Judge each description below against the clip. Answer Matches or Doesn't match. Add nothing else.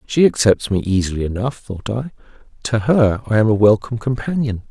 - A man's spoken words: Matches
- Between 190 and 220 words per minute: Doesn't match